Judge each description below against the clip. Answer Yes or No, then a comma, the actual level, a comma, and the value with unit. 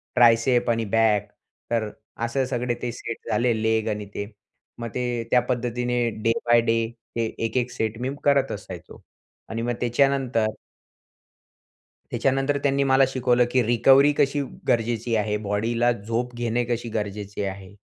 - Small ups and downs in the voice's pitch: Yes, narrow, 1.8 semitones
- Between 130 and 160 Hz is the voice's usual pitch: No, low, 120 Hz